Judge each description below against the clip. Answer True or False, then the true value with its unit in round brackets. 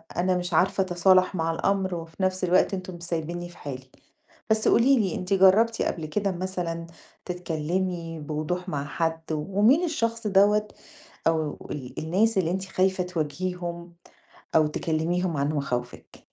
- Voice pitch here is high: False (180 Hz)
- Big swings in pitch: False (2.8 semitones)